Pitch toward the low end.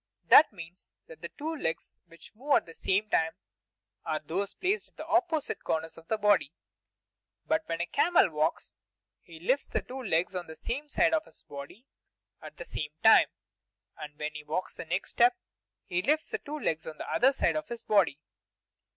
No: medium, 185 Hz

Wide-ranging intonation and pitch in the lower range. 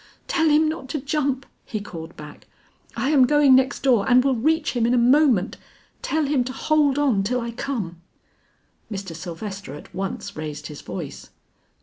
No: wide, 6.5 semitones; very high, 250 Hz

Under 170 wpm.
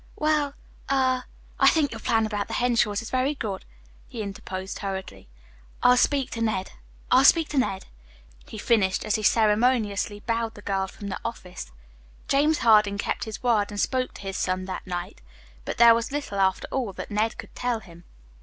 No: average, 190 wpm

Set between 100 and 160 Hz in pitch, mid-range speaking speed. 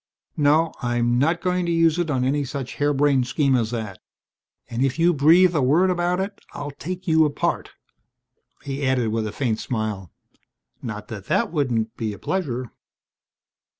Yes: medium, 140 Hz; average, 170 wpm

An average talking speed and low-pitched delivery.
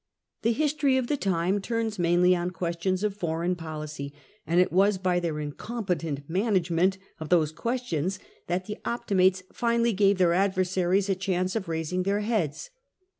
No: average, 165 wpm; medium, 185 Hz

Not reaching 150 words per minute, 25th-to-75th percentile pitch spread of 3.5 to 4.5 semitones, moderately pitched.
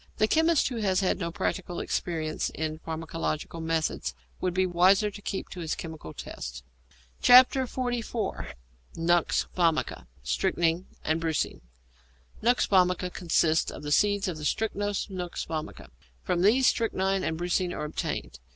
Yes: average, 140 wpm; average, 4.1 semitones; medium, 175 Hz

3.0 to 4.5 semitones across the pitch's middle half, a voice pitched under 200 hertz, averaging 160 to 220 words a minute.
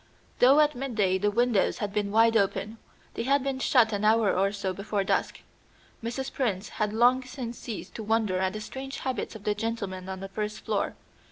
No: average, 3.5 semitones; high, 220 Hz; average, 200 wpm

